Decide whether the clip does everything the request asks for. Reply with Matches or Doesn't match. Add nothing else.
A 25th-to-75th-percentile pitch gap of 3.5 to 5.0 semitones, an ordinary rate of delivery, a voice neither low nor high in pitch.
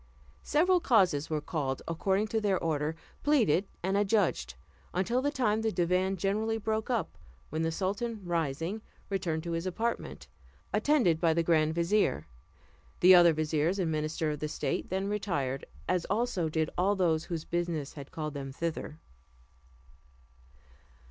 Matches